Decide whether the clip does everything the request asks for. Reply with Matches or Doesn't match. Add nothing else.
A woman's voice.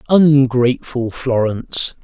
Doesn't match